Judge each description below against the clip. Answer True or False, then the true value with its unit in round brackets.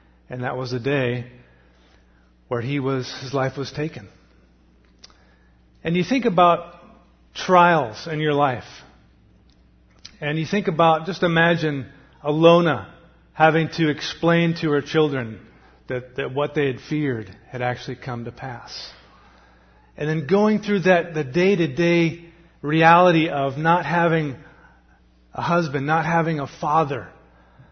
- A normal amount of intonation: False (6.9 semitones)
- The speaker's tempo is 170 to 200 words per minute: False (135 wpm)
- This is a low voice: False (145 Hz)